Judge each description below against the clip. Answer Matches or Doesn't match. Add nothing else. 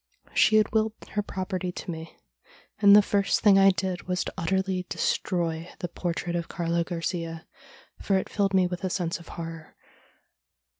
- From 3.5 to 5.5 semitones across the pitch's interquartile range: Doesn't match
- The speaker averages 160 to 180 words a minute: Matches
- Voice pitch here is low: Doesn't match